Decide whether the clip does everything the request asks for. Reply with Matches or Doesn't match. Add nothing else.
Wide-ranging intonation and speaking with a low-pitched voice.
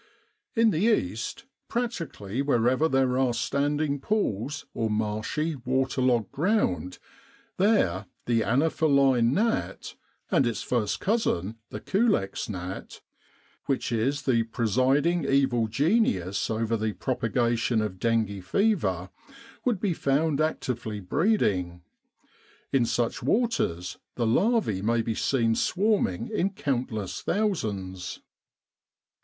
Matches